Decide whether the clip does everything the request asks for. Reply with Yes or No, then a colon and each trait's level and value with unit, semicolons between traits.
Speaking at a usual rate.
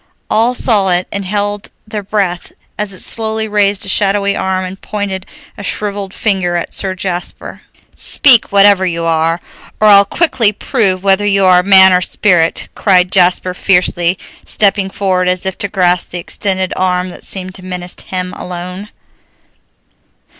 Yes: average, 160 wpm